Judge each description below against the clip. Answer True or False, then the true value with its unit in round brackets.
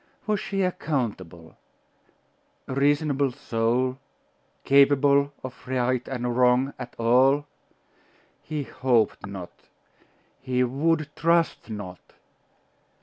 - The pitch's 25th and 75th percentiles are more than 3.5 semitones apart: False (2.9 semitones)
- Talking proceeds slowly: True (90 wpm)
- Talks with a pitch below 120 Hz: False (130 Hz)